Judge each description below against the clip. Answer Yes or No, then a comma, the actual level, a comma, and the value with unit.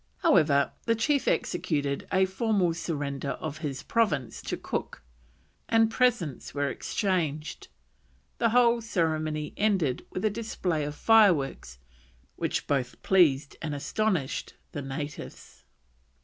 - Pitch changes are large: Yes, wide, 7.0 semitones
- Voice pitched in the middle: Yes, medium, 165 Hz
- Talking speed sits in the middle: No, slow, 120 wpm